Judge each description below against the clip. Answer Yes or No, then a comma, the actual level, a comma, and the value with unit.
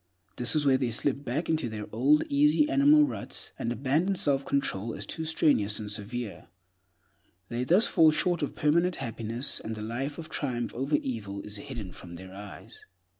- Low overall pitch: Yes, low, 130 Hz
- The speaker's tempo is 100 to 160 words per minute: No, average, 180 wpm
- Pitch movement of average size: No, wide, 5.9 semitones